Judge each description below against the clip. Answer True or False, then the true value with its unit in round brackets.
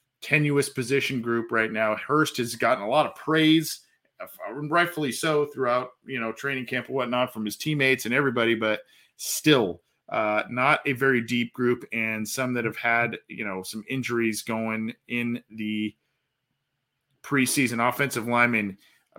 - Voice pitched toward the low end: True (125 Hz)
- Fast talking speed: False (155 wpm)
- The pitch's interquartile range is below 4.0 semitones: True (3.6 semitones)